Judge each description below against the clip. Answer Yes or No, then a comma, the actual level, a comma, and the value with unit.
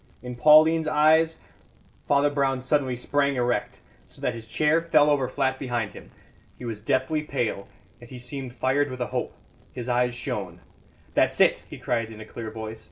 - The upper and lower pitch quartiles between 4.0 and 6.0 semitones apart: No, average, 3.3 semitones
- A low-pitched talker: Yes, low, 130 Hz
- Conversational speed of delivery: Yes, average, 185 wpm